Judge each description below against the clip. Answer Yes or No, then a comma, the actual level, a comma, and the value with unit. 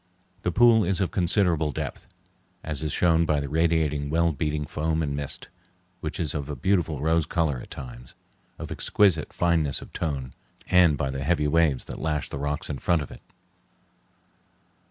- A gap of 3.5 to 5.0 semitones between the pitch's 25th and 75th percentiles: No, average, 2.7 semitones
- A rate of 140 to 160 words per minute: No, average, 175 wpm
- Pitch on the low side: Yes, very low, 80 Hz